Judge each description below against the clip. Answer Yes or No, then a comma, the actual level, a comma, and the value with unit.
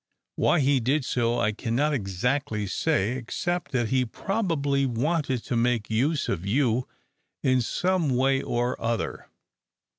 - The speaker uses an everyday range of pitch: Yes, average, 3.7 semitones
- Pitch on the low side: Yes, low, 125 Hz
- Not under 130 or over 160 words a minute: Yes, average, 140 wpm